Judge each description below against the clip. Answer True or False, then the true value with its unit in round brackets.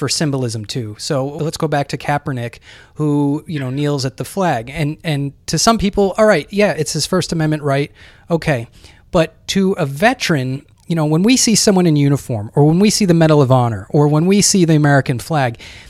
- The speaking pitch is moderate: True (150 Hz)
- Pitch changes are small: False (4.1 semitones)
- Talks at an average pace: False (215 wpm)